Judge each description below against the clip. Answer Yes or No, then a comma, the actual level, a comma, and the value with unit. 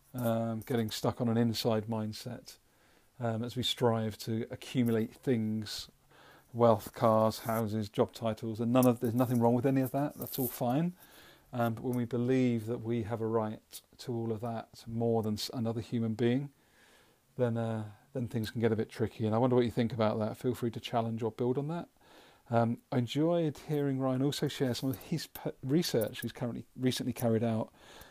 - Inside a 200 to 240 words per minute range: Yes, fast, 205 wpm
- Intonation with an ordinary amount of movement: No, narrow, 2.2 semitones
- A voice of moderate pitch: No, low, 120 Hz